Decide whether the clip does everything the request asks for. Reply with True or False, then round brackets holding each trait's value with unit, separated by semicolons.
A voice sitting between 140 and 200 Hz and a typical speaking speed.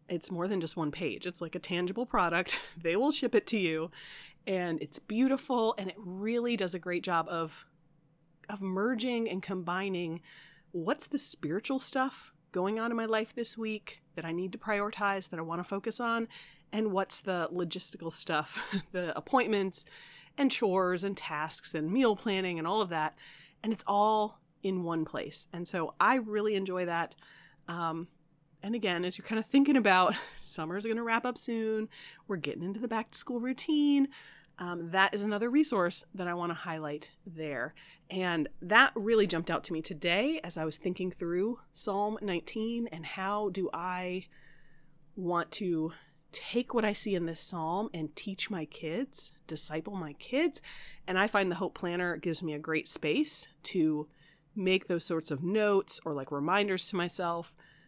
True (185 Hz; 180 wpm)